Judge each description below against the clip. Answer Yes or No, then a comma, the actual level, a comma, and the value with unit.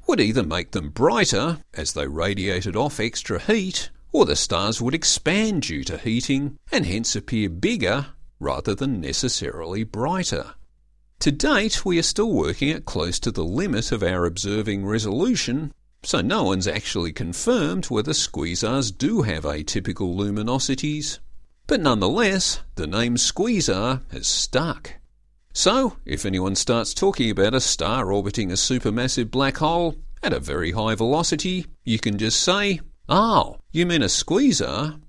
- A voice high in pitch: No, low, 115 Hz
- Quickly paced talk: No, average, 150 wpm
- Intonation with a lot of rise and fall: Yes, wide, 7.4 semitones